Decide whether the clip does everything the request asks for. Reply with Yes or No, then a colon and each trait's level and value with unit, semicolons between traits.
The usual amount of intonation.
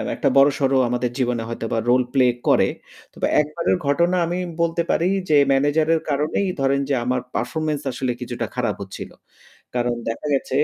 Yes: average, 3.8 semitones